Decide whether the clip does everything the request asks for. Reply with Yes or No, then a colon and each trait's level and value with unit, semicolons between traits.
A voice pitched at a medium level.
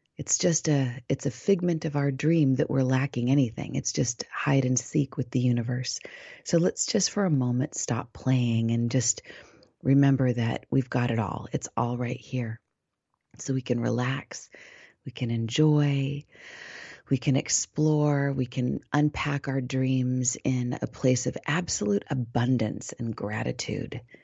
No: low, 130 Hz